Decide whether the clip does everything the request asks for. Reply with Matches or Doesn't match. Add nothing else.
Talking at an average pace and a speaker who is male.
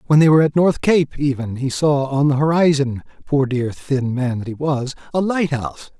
Doesn't match